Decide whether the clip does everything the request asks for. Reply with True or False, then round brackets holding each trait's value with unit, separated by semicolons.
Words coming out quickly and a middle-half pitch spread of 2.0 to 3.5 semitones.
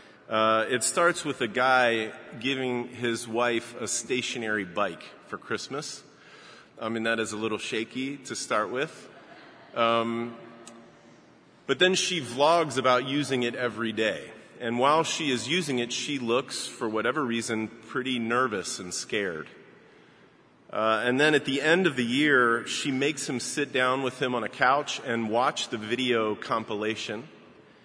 False (155 wpm; 2.7 semitones)